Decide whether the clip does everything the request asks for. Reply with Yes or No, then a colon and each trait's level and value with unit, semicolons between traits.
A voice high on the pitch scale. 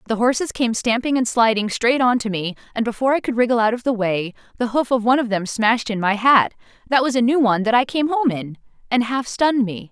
Yes: high, 235 Hz